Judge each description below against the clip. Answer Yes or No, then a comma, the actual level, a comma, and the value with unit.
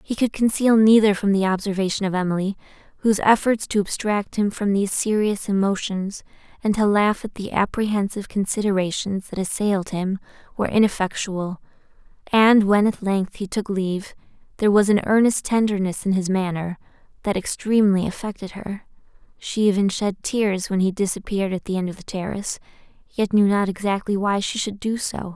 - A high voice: Yes, high, 200 Hz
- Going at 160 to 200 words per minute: Yes, average, 170 wpm